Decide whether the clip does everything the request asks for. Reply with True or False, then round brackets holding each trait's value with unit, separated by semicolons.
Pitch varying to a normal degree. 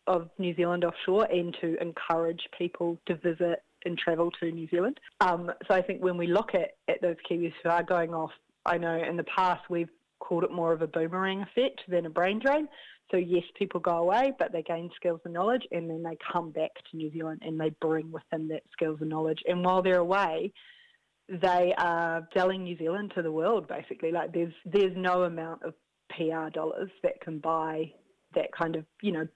False (1.9 semitones)